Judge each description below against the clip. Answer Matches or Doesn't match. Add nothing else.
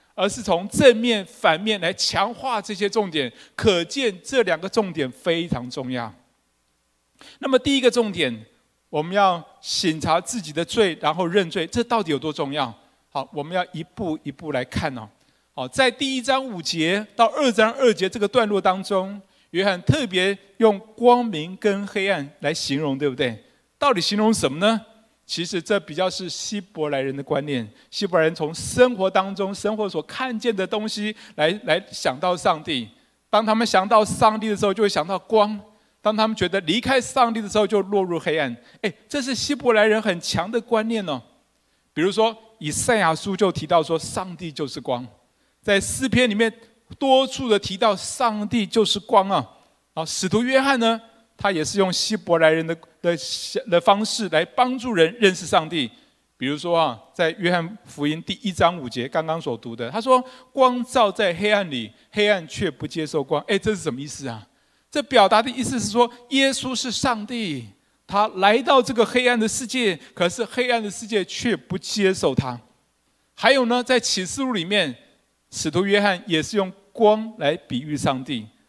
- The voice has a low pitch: Doesn't match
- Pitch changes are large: Matches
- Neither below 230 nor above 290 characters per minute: Matches